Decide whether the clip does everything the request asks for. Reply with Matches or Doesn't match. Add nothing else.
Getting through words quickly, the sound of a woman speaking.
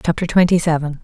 Doesn't match